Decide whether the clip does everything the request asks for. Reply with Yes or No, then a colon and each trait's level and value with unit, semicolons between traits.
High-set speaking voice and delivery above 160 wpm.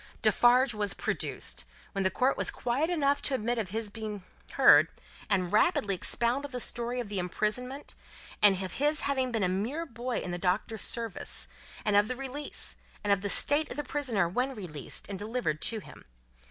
Yes: high, 225 Hz; average, 190 wpm